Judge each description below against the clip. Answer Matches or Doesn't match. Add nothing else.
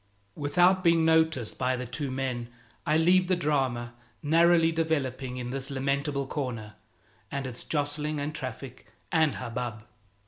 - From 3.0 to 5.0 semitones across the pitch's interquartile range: Matches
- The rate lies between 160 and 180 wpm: Doesn't match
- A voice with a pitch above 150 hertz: Doesn't match